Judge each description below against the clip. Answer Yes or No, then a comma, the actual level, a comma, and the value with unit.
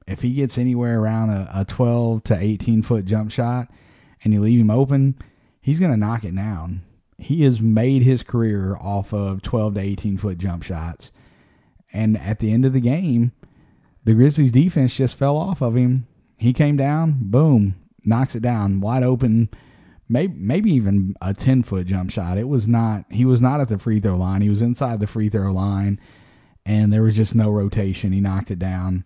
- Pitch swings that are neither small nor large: Yes, average, 3.9 semitones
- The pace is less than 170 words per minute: No, average, 200 wpm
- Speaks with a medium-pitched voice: No, low, 110 Hz